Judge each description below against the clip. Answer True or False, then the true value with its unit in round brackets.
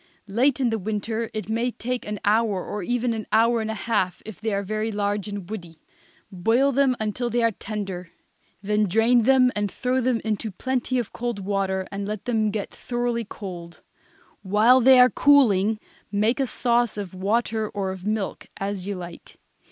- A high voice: True (215 Hz)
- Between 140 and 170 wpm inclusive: False (185 wpm)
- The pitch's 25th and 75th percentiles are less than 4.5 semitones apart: True (3.1 semitones)